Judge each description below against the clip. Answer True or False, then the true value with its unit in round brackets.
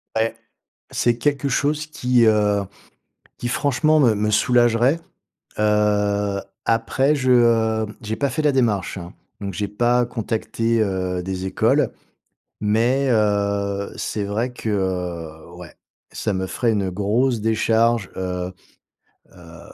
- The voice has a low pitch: True (110 Hz)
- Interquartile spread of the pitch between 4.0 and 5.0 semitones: False (3.4 semitones)